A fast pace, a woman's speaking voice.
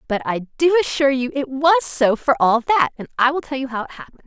Yes: fast, 265 wpm; female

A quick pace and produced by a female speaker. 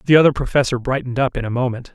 No: fast, 245 wpm; male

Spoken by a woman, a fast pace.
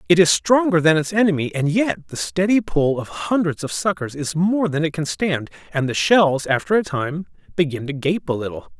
No: male; fast, 220 wpm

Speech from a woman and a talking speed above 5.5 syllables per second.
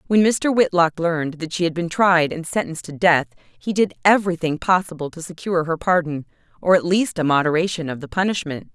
Yes: female; 5.8 syllables/s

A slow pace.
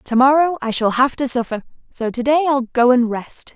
No: average, 200 wpm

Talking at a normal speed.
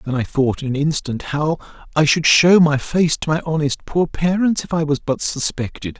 No: fast, 220 wpm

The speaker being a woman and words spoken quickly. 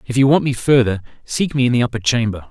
No: male; fast, 265 wpm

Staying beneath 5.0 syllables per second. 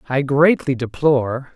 Yes: 4.4 syllables/s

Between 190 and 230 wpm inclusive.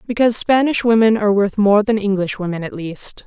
Yes: average, 200 wpm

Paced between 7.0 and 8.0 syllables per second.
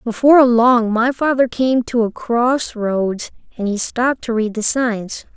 No: 4.1 syllables/s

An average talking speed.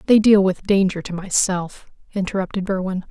Yes: average, 155 wpm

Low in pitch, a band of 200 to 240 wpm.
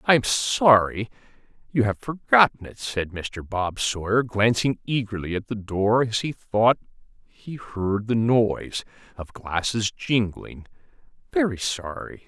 No: low, 115 Hz; slow, 135 wpm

